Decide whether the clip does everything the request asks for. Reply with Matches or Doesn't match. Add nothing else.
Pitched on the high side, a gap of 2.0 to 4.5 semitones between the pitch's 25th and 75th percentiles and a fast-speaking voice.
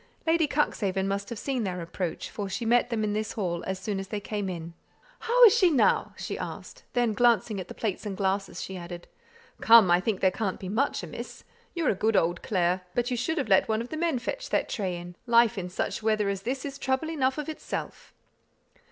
Doesn't match